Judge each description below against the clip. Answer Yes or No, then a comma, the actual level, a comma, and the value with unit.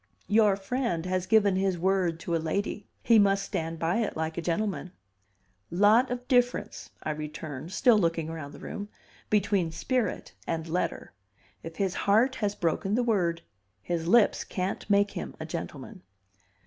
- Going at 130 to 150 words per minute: No, average, 160 wpm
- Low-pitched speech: No, high, 190 Hz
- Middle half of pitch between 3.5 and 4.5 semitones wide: Yes, average, 4.1 semitones